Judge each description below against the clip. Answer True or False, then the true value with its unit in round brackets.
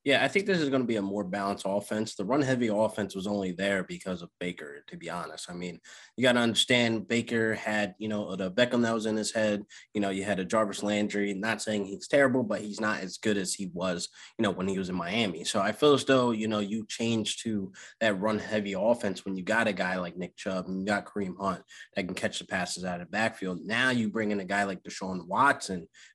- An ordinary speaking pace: False (255 wpm)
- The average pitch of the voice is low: True (105 Hz)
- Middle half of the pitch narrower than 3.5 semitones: True (2.5 semitones)